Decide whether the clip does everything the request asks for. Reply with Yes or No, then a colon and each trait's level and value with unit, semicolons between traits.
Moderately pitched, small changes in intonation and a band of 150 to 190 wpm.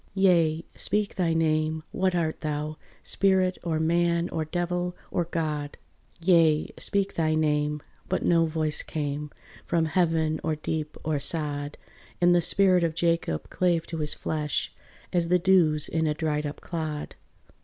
Yes: medium, 160 Hz; narrow, 2.2 semitones; average, 155 wpm